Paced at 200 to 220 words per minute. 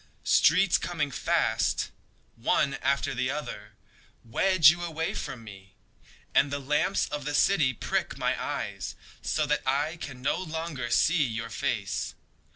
No: average, 145 wpm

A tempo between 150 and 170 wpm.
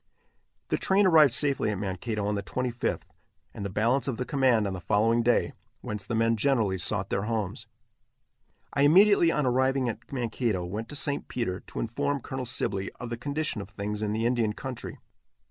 No: average, 190 wpm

